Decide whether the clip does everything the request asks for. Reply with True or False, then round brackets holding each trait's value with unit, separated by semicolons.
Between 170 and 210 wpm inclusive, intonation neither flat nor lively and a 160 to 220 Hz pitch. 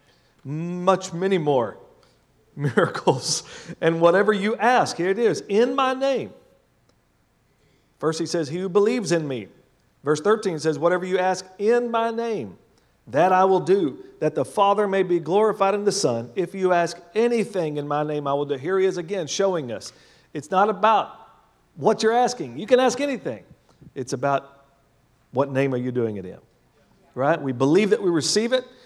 False (180 wpm; 6.1 semitones; 185 Hz)